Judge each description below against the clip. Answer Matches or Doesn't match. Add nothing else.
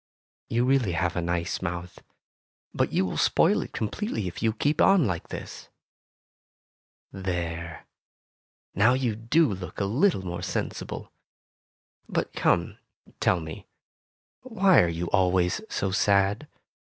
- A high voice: Doesn't match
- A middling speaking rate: Doesn't match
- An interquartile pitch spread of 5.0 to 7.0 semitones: Matches